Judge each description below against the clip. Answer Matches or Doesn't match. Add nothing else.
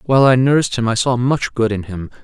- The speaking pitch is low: Matches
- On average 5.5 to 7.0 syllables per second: Matches